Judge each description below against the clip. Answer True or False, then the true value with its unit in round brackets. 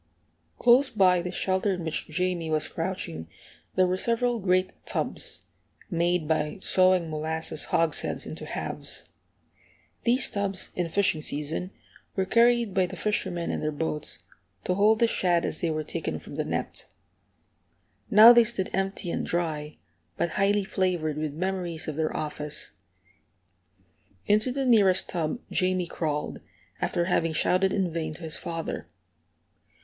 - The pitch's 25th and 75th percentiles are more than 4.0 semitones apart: False (3.4 semitones)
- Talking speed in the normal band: True (145 wpm)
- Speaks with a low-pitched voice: False (180 Hz)